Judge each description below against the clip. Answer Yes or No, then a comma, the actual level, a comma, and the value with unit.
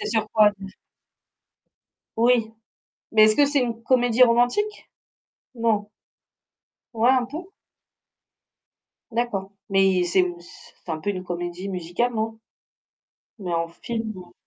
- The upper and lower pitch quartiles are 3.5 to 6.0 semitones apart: Yes, average, 4.2 semitones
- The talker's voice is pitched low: No, high, 220 Hz